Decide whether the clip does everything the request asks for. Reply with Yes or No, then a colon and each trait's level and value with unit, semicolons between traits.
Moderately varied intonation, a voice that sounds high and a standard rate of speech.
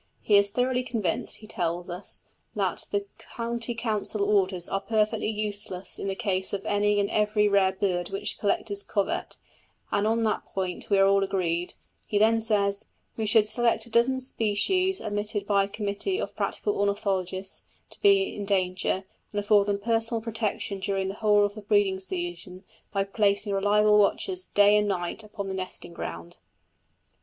No: narrow, 2.2 semitones; high, 205 Hz; average, 170 wpm